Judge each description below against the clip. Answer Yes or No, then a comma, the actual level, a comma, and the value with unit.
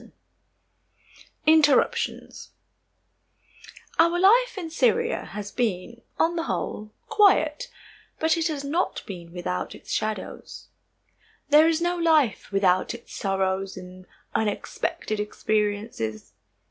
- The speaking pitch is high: Yes, high, 240 Hz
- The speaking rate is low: Yes, slow, 110 wpm